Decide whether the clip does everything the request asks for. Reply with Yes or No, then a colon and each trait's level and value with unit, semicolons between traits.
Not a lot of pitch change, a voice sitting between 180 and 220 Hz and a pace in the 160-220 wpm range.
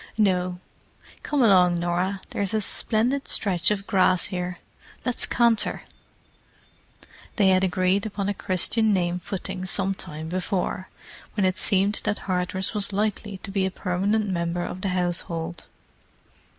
No: narrow, 2.2 semitones; high, 190 Hz; average, 140 wpm